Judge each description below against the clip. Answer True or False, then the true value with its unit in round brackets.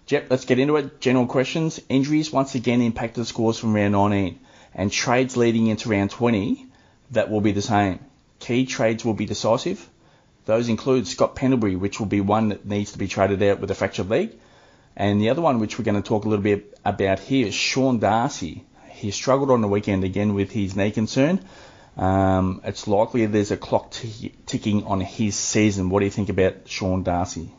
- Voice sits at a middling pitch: False (110 Hz)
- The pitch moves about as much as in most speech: True (3.9 semitones)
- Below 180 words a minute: False (205 wpm)